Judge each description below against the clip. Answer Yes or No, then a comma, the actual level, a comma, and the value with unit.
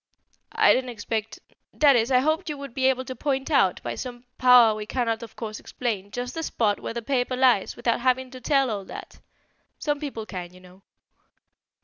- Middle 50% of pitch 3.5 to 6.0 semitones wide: No, average, 3.1 semitones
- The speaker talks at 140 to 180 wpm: No, fast, 205 wpm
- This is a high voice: Yes, high, 245 Hz